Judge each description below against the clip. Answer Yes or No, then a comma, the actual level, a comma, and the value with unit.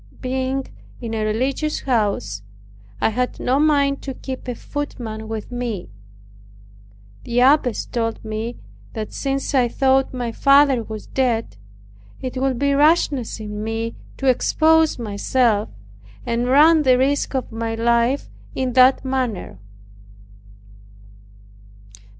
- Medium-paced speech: No, slow, 125 wpm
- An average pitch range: Yes, average, 3.2 semitones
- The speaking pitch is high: Yes, very high, 250 Hz